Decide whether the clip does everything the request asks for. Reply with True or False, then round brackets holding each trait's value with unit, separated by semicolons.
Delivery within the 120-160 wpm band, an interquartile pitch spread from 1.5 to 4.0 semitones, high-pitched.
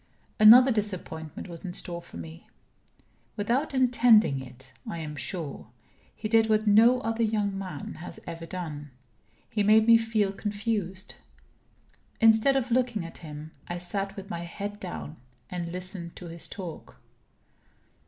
False (145 wpm; 4.8 semitones; 195 Hz)